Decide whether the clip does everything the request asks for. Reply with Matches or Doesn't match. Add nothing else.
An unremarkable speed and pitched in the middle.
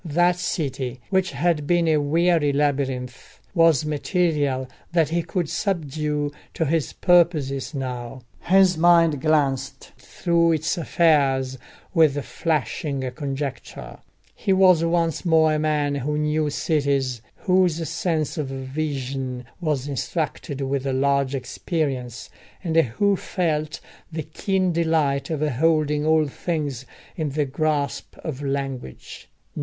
Doesn't match